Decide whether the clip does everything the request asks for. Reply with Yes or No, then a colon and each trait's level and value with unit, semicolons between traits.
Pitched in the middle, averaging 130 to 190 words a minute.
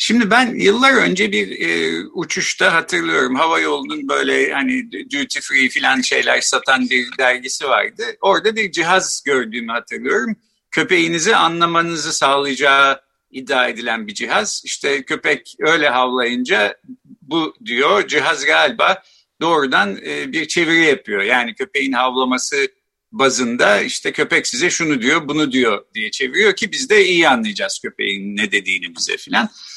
Yes: medium, 165 Hz; average, 135 wpm